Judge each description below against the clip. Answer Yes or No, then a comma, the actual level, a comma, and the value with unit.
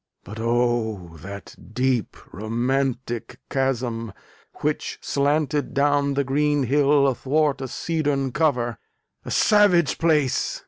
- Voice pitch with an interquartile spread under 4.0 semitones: Yes, average, 3.6 semitones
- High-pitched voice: No, low, 135 Hz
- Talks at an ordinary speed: No, slow, 105 wpm